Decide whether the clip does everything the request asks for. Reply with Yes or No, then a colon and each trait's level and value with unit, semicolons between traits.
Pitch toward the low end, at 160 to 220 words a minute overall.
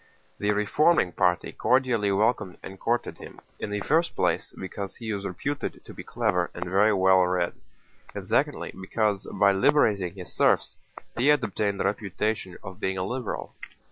Yes: low, 100 Hz; average, 170 wpm